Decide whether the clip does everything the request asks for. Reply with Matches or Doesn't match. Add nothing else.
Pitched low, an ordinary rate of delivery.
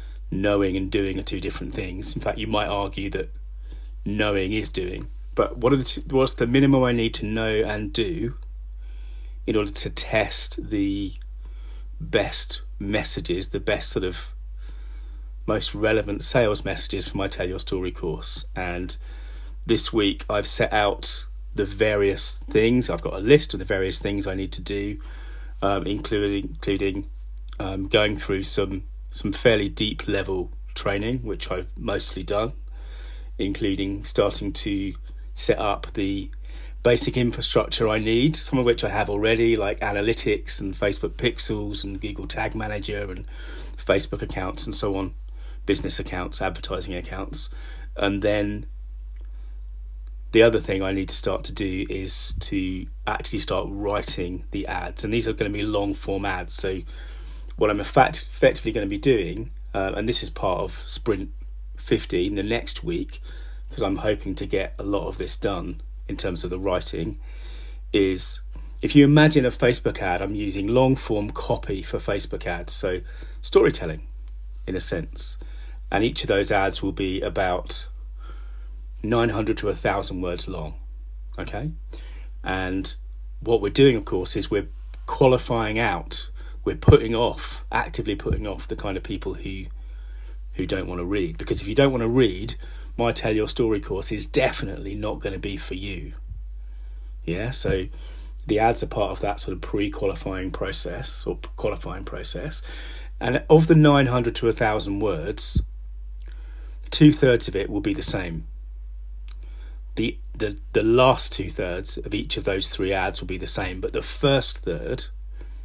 Matches